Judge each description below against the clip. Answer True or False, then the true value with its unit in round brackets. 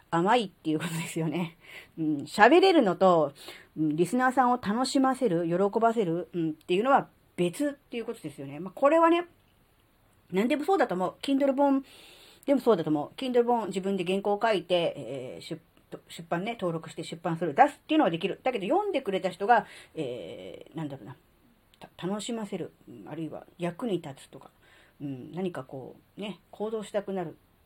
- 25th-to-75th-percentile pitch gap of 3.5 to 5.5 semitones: False (7.1 semitones)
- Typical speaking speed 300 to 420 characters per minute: True (385 characters per minute)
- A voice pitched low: False (190 Hz)